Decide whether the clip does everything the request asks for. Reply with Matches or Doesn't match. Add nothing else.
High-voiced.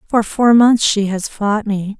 Matches